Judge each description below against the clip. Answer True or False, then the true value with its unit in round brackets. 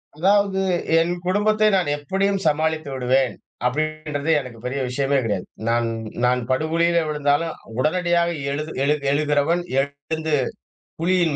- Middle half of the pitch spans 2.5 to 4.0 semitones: True (3.4 semitones)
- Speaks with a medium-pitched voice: True (155 Hz)